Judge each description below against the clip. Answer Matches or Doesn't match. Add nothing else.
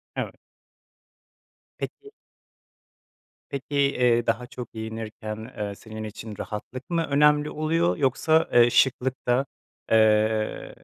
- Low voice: Matches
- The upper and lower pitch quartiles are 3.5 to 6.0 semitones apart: Matches